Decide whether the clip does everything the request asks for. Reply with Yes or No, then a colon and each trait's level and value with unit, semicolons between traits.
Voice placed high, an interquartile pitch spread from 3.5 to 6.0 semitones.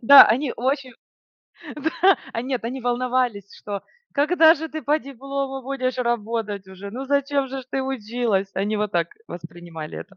Yes: very high, 250 Hz; average, 4.8 semitones